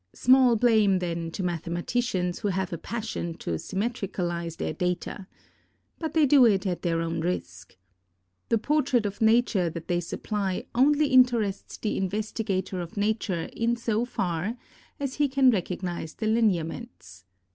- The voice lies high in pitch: Yes, high, 200 Hz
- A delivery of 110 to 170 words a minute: Yes, average, 145 wpm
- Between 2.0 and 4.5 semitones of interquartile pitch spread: No, average, 5.3 semitones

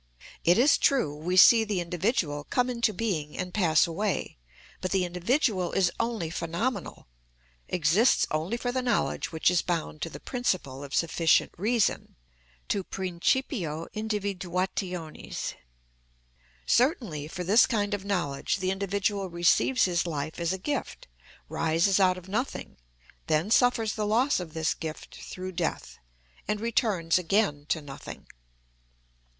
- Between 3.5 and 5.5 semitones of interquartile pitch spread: Yes, average, 4.7 semitones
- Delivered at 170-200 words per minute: No, average, 140 wpm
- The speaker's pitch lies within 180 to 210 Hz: Yes, medium, 185 Hz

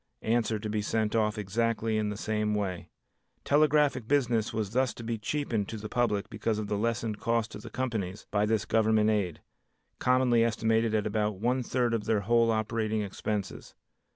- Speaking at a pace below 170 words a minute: No, average, 180 wpm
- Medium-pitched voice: No, low, 110 Hz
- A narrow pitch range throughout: Yes, narrow, 1.7 semitones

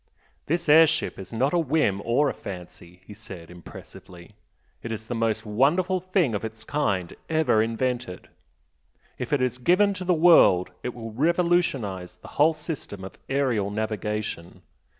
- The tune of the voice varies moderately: No, wide, 7.7 semitones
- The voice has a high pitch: No, low, 120 Hz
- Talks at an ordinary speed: Yes, average, 160 wpm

